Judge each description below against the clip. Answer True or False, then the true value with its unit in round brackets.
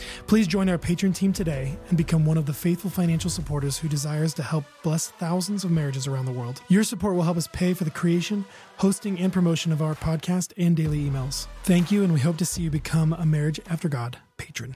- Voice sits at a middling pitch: True (165 Hz)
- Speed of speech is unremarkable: False (230 wpm)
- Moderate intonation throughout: True (3.1 semitones)